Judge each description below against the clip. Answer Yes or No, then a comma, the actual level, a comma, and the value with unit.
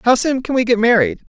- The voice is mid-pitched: No, high, 240 Hz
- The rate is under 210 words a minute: No, fast, 275 wpm